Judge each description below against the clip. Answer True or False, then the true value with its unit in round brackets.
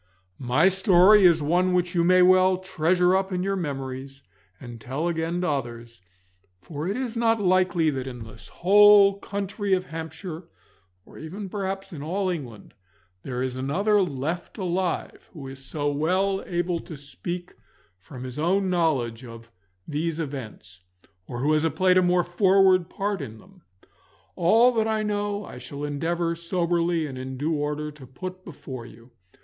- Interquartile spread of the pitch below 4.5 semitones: False (5.0 semitones)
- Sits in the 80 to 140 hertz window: False (170 Hz)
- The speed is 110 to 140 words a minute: False (165 wpm)